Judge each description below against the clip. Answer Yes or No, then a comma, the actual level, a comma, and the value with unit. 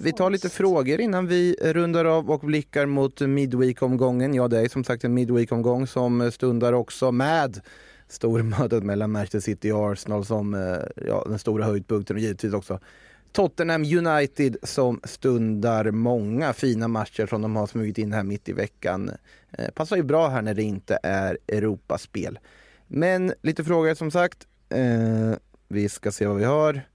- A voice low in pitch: Yes, low, 120 Hz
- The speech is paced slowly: No, average, 165 wpm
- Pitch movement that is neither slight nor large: No, wide, 5.7 semitones